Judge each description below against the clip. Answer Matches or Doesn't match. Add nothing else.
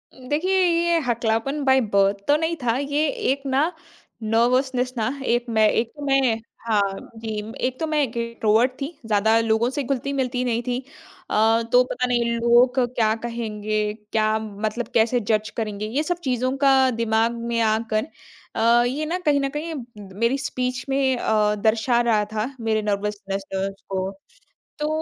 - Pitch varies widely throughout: Doesn't match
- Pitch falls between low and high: Doesn't match